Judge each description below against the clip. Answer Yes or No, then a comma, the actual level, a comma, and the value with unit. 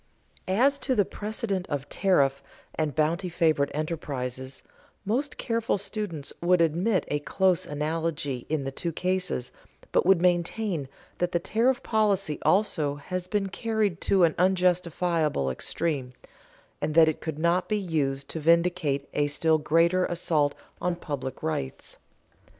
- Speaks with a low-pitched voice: No, medium, 170 Hz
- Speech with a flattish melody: No, average, 4.3 semitones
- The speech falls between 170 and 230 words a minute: No, average, 140 wpm